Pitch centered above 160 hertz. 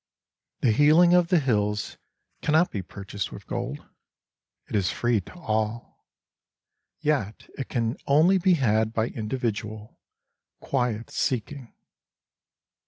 No: low, 120 Hz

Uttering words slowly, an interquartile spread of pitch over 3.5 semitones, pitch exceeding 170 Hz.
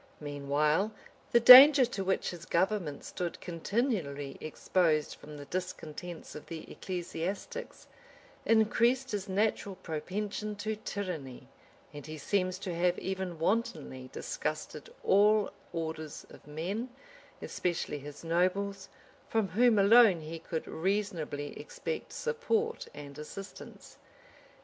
Yes: slow, 115 wpm; average, 5.3 semitones; medium, 185 Hz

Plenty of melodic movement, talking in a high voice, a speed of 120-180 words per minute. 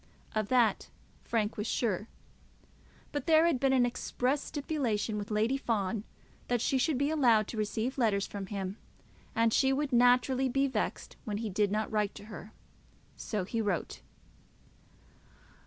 No: average, 4.0 semitones; high, 230 Hz; average, 155 wpm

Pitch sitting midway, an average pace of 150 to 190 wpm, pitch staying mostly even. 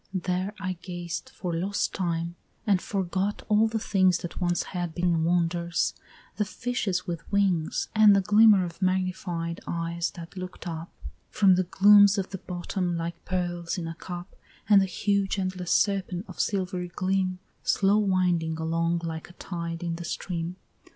Yes: medium, 180 Hz; average, 165 wpm; narrow, 2.3 semitones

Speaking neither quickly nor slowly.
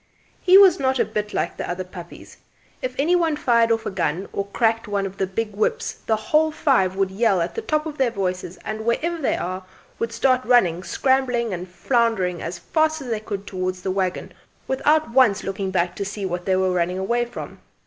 No: fast, 215 wpm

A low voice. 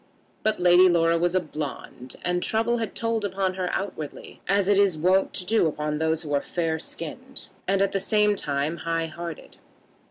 No: medium, 180 Hz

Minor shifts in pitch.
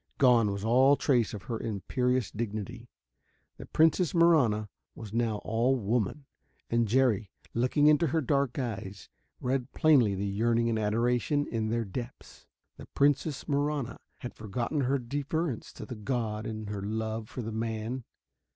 No: average, 3.8 semitones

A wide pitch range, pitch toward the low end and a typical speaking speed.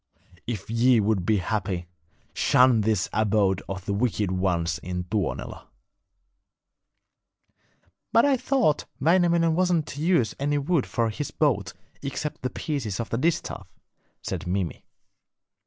No: wide, 7.5 semitones; low, 115 Hz; slow, 130 wpm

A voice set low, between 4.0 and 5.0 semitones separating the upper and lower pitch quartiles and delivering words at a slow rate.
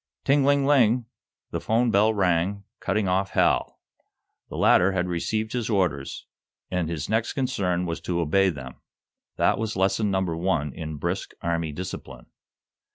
No: very low, 95 Hz; average, 4.6 semitones; average, 155 wpm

